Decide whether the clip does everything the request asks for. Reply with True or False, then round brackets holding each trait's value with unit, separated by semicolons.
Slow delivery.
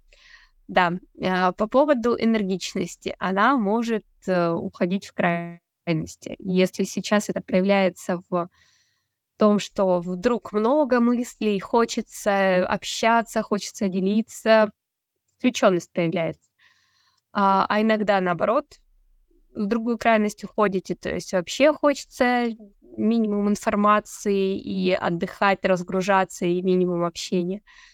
True (95 wpm)